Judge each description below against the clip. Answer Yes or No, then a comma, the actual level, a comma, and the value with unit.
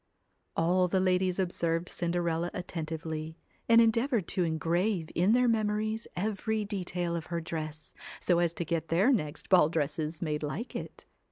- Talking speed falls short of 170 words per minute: Yes, average, 155 wpm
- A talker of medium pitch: Yes, medium, 175 Hz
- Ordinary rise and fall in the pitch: Yes, average, 3.8 semitones